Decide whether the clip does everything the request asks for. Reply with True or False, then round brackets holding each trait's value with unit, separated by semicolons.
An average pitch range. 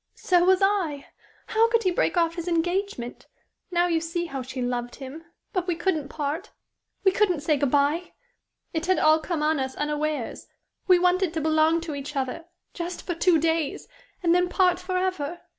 True (3.4 semitones)